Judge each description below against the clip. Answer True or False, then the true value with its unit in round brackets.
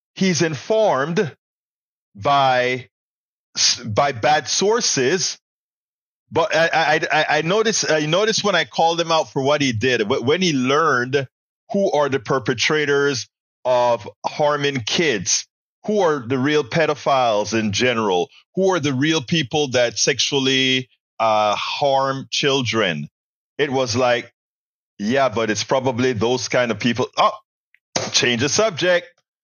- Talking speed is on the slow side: True (130 wpm)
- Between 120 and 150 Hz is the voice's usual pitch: True (140 Hz)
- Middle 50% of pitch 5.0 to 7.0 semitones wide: False (4.3 semitones)